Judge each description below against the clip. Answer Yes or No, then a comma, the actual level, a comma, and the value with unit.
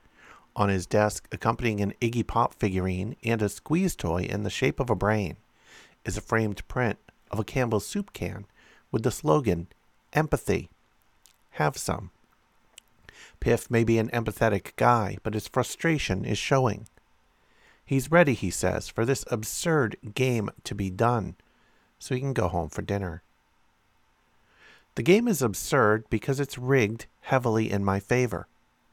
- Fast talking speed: No, average, 150 wpm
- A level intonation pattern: No, average, 3.9 semitones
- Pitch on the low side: Yes, low, 110 Hz